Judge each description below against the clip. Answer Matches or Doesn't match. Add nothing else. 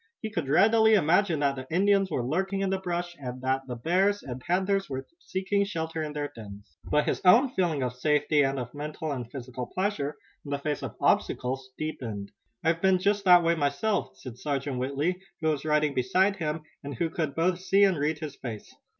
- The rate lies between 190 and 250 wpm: Matches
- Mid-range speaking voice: Matches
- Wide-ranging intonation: Matches